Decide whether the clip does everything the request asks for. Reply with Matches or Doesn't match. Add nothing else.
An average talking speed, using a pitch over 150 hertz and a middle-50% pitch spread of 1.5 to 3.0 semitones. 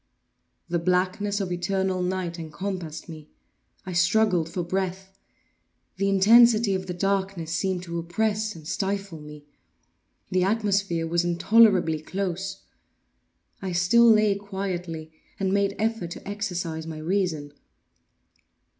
Doesn't match